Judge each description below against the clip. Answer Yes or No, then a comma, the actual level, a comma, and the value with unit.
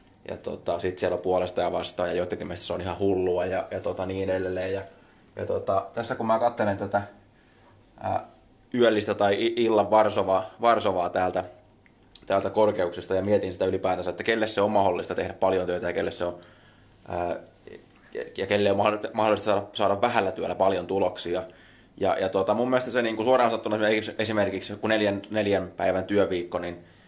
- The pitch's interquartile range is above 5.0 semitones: No, narrow, 2.6 semitones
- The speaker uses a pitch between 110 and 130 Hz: No, low, 100 Hz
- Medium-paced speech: No, fast, 175 wpm